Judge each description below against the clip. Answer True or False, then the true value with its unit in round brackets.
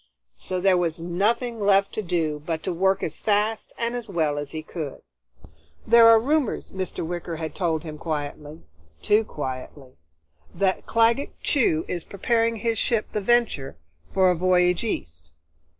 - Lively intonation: True (5.8 semitones)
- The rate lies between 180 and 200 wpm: False (160 wpm)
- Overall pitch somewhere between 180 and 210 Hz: True (185 Hz)